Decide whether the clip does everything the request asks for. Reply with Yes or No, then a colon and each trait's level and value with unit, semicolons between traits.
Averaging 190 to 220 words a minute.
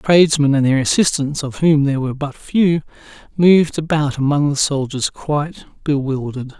No: average, 155 wpm